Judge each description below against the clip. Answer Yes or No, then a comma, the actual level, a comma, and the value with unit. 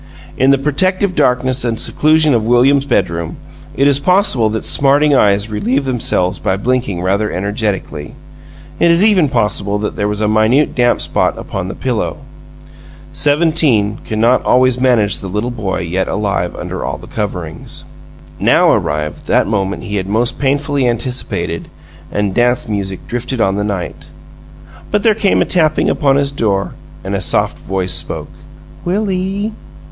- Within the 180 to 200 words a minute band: No, average, 160 wpm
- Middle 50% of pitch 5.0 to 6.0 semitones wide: Yes, wide, 5.6 semitones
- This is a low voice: Yes, low, 120 Hz